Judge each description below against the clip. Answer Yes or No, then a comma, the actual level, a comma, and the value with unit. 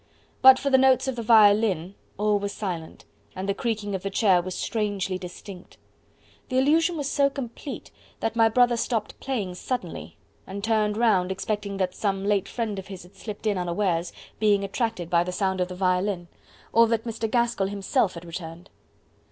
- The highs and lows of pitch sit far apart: No, average, 3.7 semitones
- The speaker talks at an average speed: Yes, average, 185 wpm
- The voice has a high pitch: Yes, high, 205 Hz